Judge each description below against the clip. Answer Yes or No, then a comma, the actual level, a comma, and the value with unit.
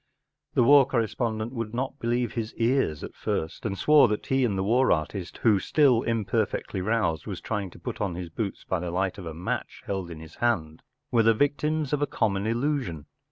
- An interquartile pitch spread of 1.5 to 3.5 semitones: No, average, 4.8 semitones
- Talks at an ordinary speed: No, fast, 210 wpm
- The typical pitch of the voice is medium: No, low, 110 Hz